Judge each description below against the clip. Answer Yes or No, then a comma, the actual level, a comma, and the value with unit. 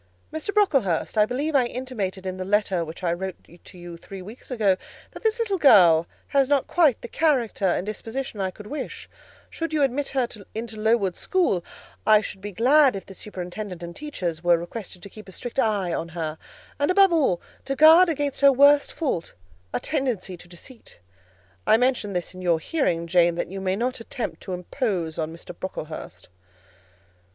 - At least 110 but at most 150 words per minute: No, average, 190 wpm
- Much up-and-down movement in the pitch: Yes, wide, 7.2 semitones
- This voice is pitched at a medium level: No, high, 210 Hz